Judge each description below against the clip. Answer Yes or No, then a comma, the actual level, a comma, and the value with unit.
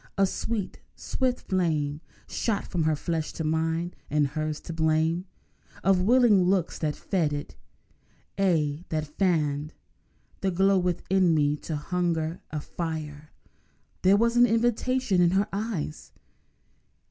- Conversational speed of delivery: No, slow, 130 wpm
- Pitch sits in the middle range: Yes, medium, 170 Hz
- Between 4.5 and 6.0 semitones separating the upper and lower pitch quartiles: No, average, 3.9 semitones